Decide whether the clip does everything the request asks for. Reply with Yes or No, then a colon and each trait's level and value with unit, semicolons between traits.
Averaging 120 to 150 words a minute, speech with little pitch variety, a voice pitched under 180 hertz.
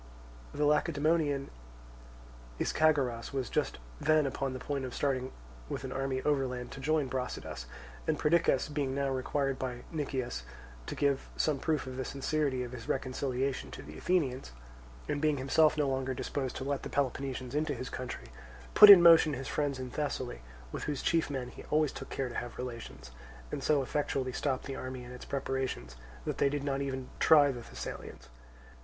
No: average, 180 wpm; narrow, 2.3 semitones; low, 135 Hz